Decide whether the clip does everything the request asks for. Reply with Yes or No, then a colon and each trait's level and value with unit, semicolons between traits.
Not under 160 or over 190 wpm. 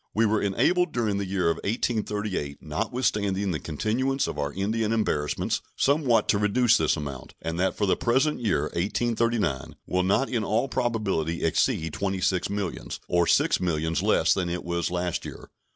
Yes: average, 170 wpm